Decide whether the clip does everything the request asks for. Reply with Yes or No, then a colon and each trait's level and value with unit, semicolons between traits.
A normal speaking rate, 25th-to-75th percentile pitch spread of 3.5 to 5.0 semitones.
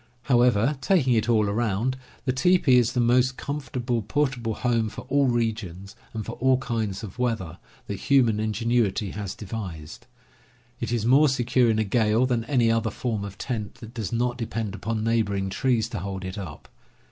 No: average, 185 wpm; average, 3.1 semitones